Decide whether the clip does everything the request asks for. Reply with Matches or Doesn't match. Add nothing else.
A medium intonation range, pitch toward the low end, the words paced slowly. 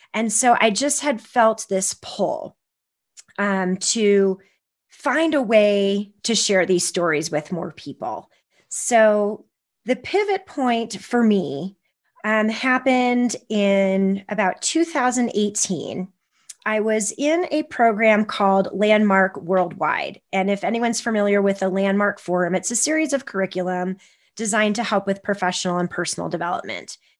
Doesn't match